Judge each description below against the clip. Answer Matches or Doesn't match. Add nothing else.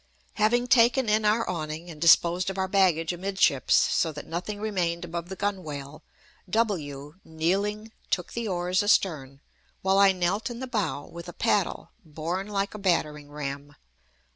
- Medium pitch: Matches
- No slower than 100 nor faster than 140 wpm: Doesn't match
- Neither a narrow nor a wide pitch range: Matches